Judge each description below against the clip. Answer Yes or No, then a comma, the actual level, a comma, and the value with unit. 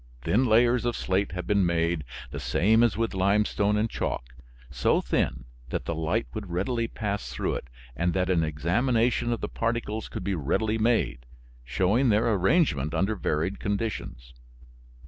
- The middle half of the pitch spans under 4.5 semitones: No, average, 5.2 semitones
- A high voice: No, low, 100 Hz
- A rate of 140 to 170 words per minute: Yes, average, 165 wpm